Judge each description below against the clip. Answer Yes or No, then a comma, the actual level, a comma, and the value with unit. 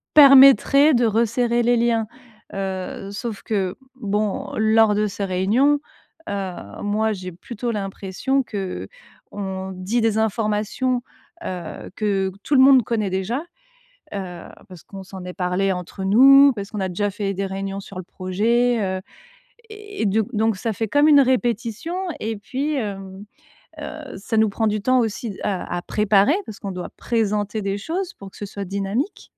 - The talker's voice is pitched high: Yes, high, 210 Hz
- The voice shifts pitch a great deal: No, average, 3.6 semitones